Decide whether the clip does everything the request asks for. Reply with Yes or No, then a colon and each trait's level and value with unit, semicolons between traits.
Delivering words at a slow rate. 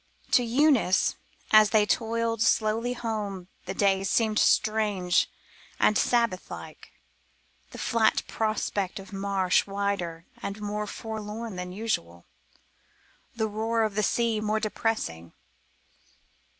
Yes: slow, 115 wpm